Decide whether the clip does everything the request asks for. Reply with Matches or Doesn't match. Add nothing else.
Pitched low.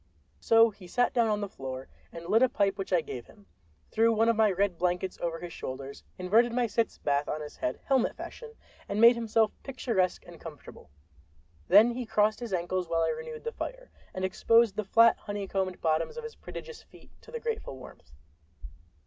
Doesn't match